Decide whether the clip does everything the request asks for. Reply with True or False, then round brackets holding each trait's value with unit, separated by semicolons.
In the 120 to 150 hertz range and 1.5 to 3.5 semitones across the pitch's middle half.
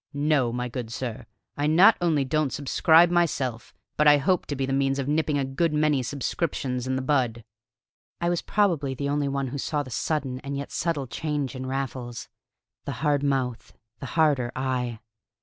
True (140 Hz; 2.8 semitones)